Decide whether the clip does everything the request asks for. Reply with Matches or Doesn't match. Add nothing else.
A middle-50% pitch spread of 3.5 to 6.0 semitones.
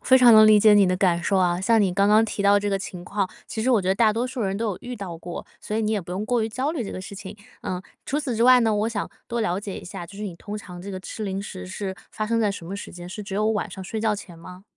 Doesn't match